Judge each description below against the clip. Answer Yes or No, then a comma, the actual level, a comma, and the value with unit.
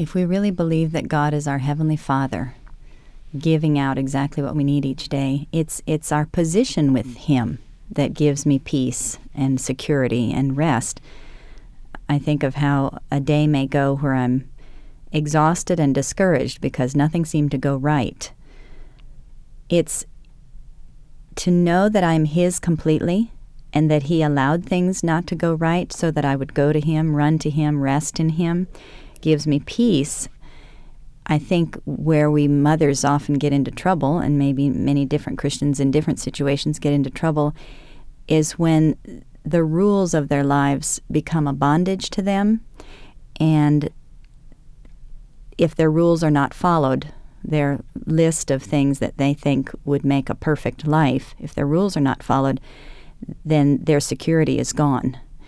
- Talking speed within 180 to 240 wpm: No, average, 155 wpm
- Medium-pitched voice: Yes, medium, 150 Hz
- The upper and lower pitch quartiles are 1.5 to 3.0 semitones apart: Yes, narrow, 2.5 semitones